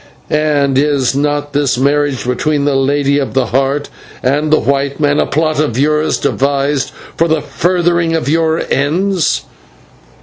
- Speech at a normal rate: Yes, average, 155 wpm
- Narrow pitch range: Yes, narrow, 1.9 semitones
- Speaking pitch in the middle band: Yes, medium, 145 Hz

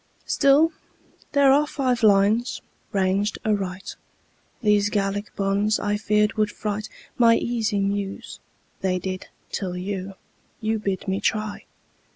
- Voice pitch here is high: Yes, high, 205 Hz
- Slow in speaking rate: Yes, slow, 125 wpm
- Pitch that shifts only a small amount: Yes, narrow, 2.0 semitones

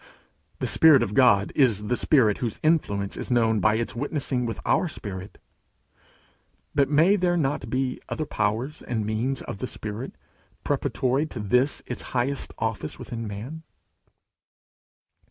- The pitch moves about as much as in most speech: Yes, average, 4.7 semitones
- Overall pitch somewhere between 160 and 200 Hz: No, low, 125 Hz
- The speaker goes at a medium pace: Yes, average, 145 wpm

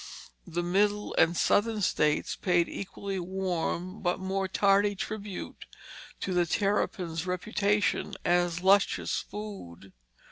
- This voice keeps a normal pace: No, slow, 110 wpm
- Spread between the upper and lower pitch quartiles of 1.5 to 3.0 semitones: Yes, narrow, 2.5 semitones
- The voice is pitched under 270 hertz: Yes, high, 190 Hz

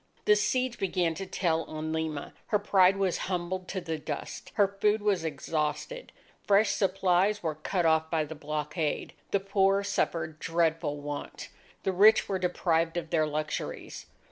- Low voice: No, medium, 175 Hz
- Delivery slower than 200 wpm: Yes, average, 160 wpm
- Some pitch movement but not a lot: Yes, average, 3.7 semitones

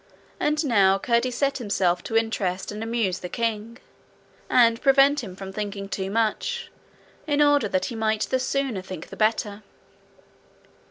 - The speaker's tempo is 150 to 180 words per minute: Yes, average, 155 wpm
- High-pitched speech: Yes, high, 225 Hz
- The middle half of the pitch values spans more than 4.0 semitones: Yes, average, 4.6 semitones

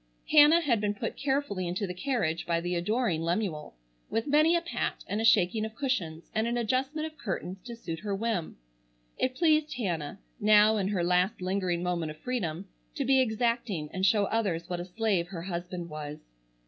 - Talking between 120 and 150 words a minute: No, average, 190 wpm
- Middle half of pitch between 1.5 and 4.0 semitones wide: No, wide, 5.5 semitones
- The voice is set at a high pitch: Yes, high, 205 Hz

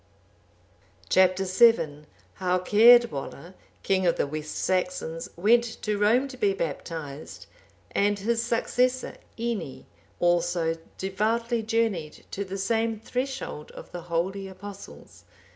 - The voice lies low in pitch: No, high, 195 Hz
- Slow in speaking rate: Yes, slow, 115 wpm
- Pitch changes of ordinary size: Yes, average, 4.8 semitones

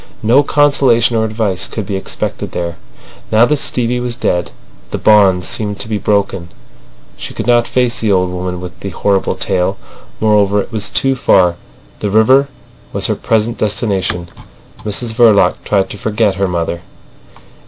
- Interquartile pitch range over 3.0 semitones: Yes, average, 3.7 semitones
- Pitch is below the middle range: Yes, low, 105 Hz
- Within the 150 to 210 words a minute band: Yes, average, 165 wpm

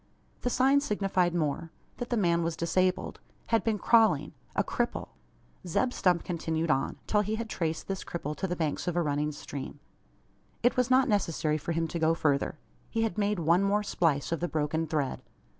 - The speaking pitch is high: No, medium, 170 Hz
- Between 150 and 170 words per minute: No, average, 190 wpm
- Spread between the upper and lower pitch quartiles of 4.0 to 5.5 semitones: Yes, average, 4.9 semitones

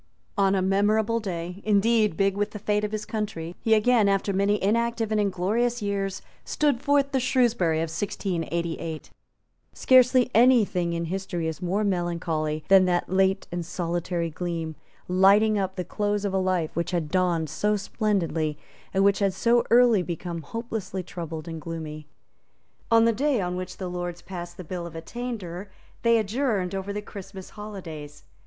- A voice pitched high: Yes, high, 195 Hz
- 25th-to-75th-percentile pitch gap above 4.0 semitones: No, average, 3.7 semitones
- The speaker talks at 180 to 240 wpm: No, average, 170 wpm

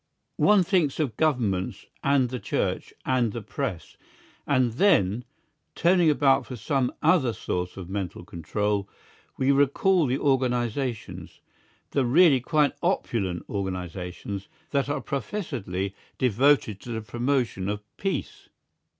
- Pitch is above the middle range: No, low, 125 Hz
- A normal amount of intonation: No, wide, 5.8 semitones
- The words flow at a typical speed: No, slow, 125 wpm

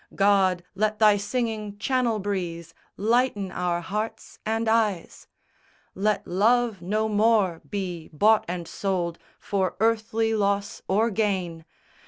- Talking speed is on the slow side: Yes, slow, 120 wpm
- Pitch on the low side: No, high, 205 Hz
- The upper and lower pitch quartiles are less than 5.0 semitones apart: Yes, average, 3.0 semitones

